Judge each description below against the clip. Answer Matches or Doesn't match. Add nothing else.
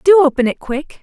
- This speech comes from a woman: Matches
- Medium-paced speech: Doesn't match